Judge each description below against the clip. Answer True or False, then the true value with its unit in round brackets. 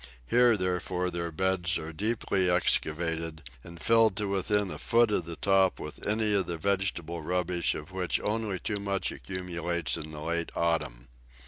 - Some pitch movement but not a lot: True (3.0 semitones)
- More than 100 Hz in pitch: False (90 Hz)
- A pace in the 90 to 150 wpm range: False (165 wpm)